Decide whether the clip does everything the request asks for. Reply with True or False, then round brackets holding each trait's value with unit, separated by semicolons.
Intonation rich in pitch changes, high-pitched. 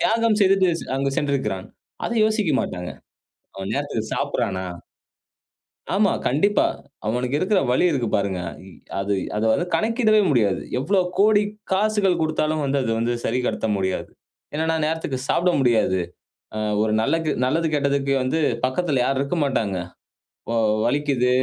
False (7.3 semitones; 140 Hz)